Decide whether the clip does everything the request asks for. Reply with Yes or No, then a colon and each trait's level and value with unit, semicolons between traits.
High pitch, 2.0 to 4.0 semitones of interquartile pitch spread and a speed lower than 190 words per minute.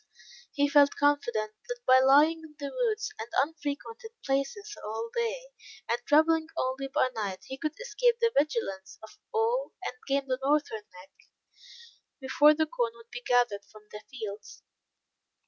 No: very high, 280 Hz; wide, 5.5 semitones; average, 160 wpm